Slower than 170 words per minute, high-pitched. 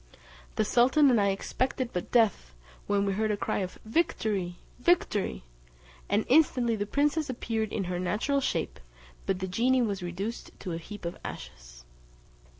Yes: average, 160 wpm; high, 210 Hz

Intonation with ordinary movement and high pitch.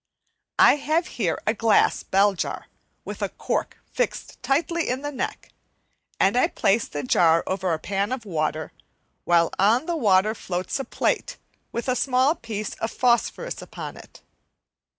No: wide, 6.1 semitones; high, 220 Hz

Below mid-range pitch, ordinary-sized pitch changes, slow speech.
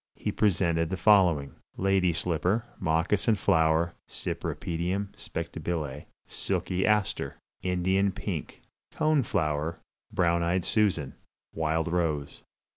Yes: very low, 85 Hz; average, 3.2 semitones; slow, 100 wpm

